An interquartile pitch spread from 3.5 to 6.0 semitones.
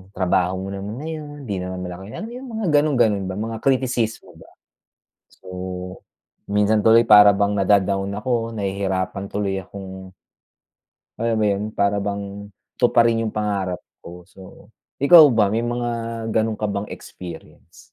No: average, 2.9 semitones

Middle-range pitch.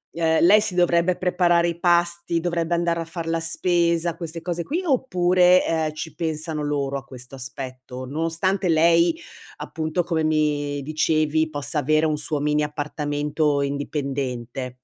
Yes: medium, 160 Hz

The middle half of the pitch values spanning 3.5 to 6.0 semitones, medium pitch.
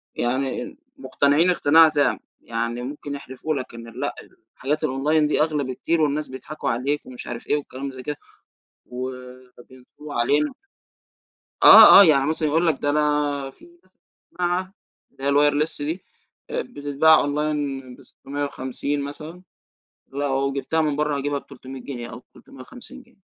No: narrow, 2.6 semitones; medium, 145 Hz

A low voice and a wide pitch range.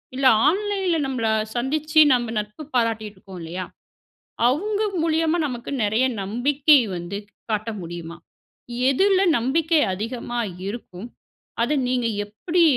No: high, 245 Hz; wide, 6.7 semitones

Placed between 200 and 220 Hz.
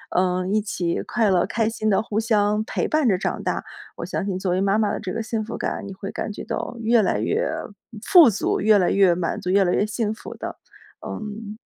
Yes: high, 210 Hz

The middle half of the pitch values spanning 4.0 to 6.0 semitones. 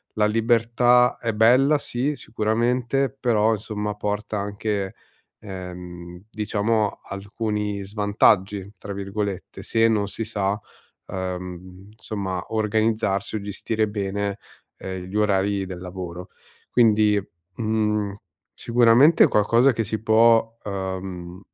No: narrow, 2.5 semitones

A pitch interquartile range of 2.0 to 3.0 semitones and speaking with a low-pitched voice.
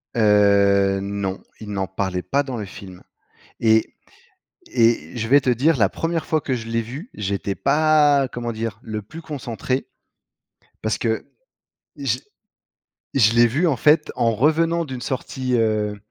No: average, 5.1 semitones; low, 115 Hz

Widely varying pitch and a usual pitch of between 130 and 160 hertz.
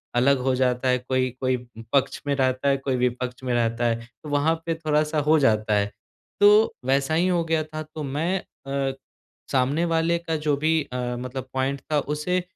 No: average, 3.5 semitones; medium, 140 Hz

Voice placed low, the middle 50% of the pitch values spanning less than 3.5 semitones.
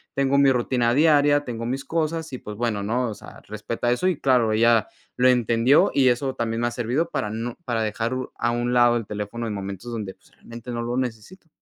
Yes: low, 120 Hz; narrow, 2.5 semitones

